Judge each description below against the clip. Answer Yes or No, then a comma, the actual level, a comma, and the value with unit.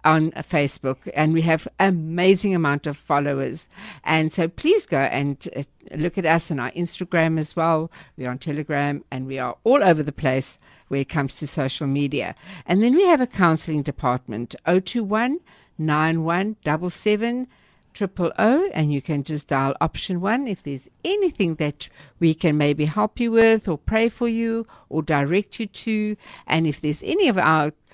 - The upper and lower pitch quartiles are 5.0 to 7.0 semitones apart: Yes, wide, 5.4 semitones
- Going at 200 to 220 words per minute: No, average, 185 wpm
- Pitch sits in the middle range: Yes, medium, 160 Hz